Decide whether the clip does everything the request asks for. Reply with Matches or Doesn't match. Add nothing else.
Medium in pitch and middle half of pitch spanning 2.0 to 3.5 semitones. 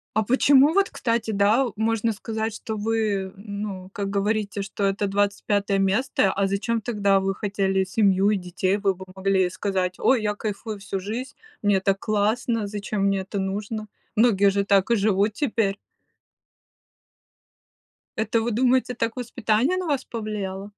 Doesn't match